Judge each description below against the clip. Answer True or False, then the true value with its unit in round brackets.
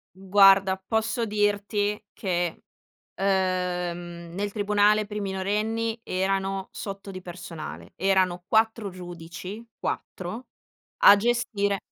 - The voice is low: False (195 Hz)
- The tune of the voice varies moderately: False (2.2 semitones)